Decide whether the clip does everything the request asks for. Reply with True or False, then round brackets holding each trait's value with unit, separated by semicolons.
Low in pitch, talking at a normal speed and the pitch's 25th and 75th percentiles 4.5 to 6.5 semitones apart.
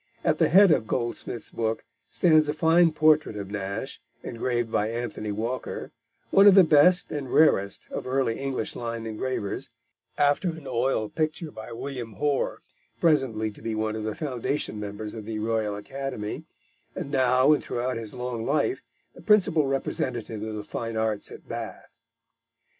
True (120 Hz; 165 wpm; 4.9 semitones)